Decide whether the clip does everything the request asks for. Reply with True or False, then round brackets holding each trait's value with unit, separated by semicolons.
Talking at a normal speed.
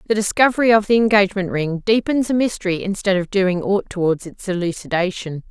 True (175 wpm)